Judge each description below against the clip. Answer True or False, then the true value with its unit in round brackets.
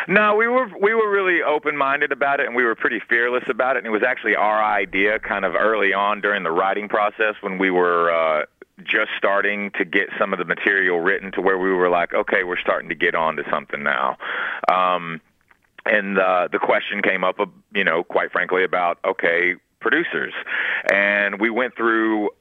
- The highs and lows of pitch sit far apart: True (6.5 semitones)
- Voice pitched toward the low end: True (105 Hz)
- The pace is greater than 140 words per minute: True (200 wpm)